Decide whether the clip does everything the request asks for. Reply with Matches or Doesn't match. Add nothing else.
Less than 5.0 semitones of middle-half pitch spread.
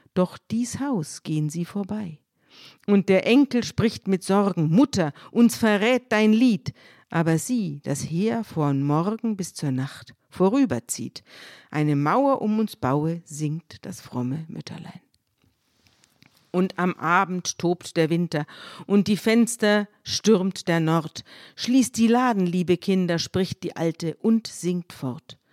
Doesn't match